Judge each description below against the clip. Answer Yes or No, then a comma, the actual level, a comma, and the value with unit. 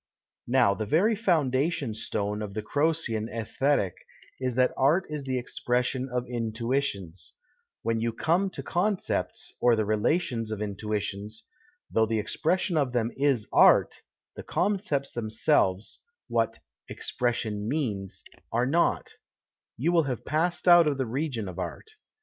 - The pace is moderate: Yes, average, 145 wpm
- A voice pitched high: No, low, 125 Hz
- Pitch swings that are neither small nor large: No, wide, 5.9 semitones